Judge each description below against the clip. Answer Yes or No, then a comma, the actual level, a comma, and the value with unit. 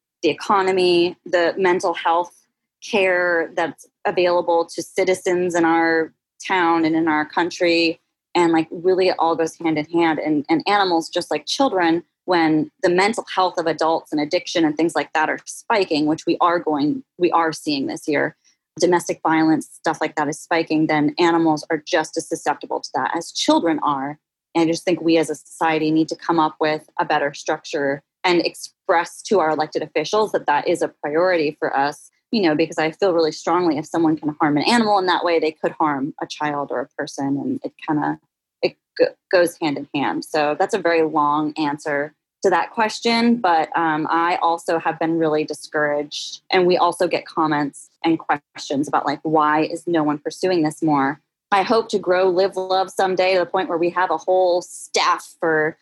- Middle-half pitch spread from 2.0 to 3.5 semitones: Yes, narrow, 2.6 semitones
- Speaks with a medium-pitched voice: Yes, medium, 165 Hz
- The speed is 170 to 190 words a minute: No, average, 200 wpm